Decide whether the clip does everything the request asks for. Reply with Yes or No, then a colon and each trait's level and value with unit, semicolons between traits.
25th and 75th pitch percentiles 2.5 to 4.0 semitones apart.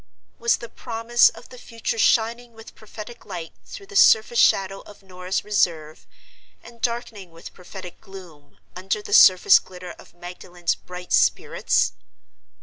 No: average, 4.4 semitones